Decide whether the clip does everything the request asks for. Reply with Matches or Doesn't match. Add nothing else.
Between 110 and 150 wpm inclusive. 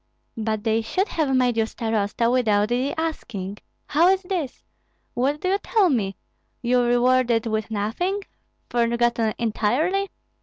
Matches